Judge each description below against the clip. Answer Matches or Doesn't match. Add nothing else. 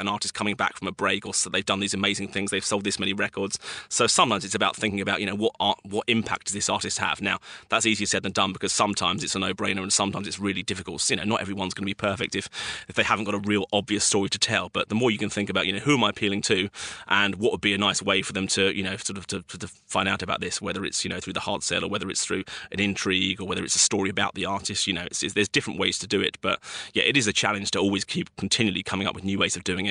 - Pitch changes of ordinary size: Doesn't match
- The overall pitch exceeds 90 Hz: Matches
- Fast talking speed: Matches